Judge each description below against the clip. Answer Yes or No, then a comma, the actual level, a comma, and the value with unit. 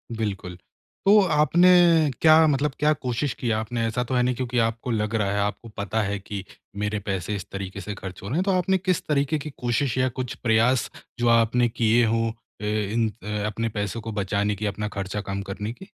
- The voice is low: Yes, low, 115 Hz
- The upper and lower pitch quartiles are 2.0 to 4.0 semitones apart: No, average, 4.4 semitones